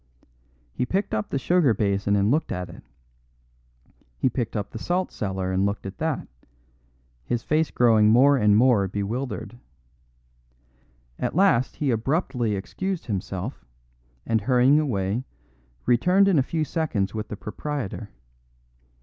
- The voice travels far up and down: Yes, wide, 6.3 semitones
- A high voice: No, low, 120 Hz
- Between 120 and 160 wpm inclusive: Yes, average, 140 wpm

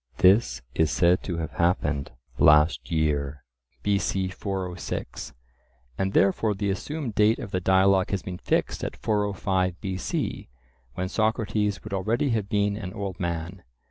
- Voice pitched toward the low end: Yes, very low, 95 Hz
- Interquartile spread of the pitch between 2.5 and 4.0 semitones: Yes, average, 2.8 semitones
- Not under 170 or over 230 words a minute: No, average, 140 wpm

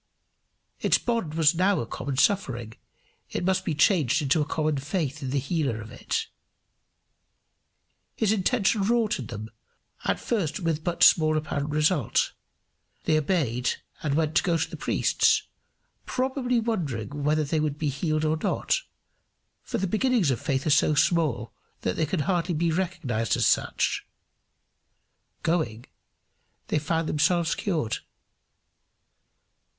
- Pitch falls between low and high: Yes, medium, 155 Hz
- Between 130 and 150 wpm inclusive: Yes, average, 145 wpm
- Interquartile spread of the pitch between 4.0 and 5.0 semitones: Yes, average, 4.6 semitones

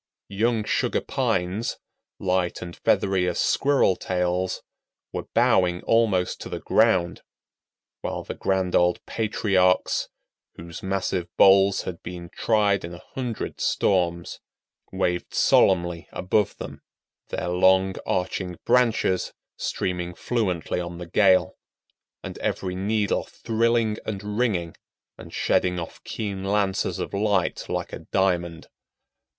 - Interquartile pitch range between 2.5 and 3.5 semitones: Yes, average, 2.8 semitones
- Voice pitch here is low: Yes, very low, 95 Hz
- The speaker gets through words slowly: Yes, slow, 120 wpm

